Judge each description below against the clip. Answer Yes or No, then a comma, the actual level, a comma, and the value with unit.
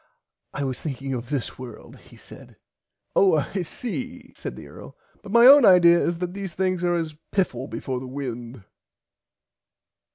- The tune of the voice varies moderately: No, wide, 6.6 semitones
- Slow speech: No, average, 165 wpm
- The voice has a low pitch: No, medium, 170 Hz